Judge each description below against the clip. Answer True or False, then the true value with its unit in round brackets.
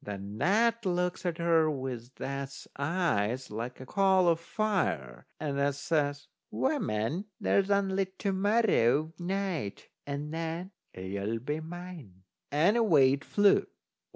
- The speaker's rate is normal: False (130 wpm)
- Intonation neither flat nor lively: False (6.4 semitones)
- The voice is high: False (155 Hz)